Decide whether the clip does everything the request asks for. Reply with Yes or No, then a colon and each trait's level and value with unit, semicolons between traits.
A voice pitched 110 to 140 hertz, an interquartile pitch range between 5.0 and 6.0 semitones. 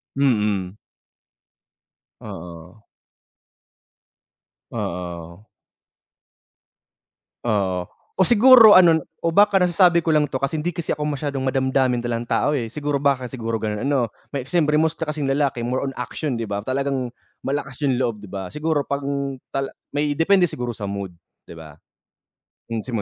Yes: low, 135 Hz; average, 5.3 semitones